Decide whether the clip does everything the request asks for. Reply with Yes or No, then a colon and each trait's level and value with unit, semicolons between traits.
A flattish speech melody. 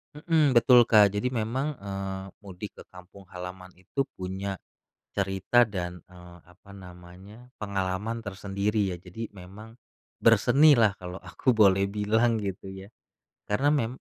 No: average, 3.1 semitones